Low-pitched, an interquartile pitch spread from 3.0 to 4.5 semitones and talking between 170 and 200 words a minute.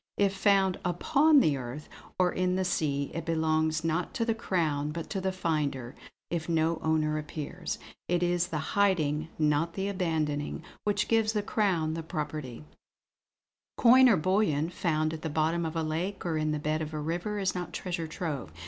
No: medium, 165 Hz; average, 3.4 semitones; average, 185 wpm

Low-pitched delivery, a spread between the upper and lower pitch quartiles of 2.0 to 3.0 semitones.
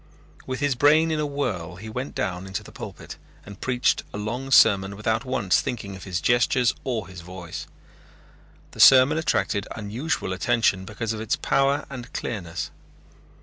No: low, 110 Hz; average, 5.3 semitones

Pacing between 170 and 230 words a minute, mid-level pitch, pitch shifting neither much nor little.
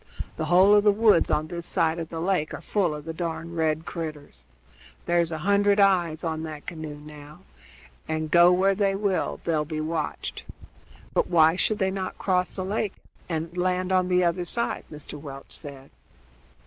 Yes: average, 185 wpm; medium, 170 Hz; average, 3.0 semitones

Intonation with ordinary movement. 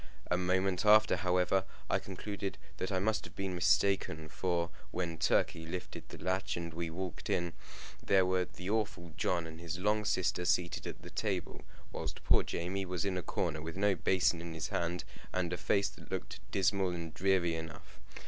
No: narrow, 2.2 semitones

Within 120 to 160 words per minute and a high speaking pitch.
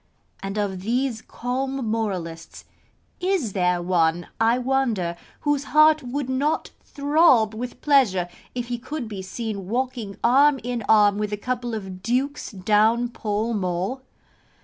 Yes: average, 140 wpm; high, 230 Hz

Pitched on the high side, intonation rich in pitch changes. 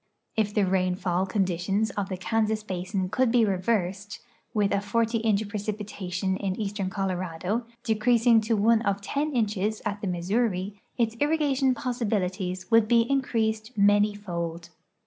No: high, 205 Hz; average, 3.2 semitones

